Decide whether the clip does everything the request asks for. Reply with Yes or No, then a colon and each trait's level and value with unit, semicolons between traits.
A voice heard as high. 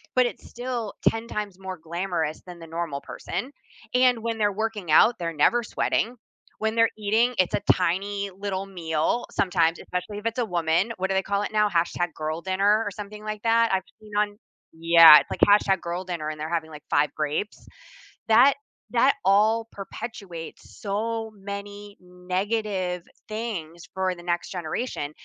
Yes: high, 195 Hz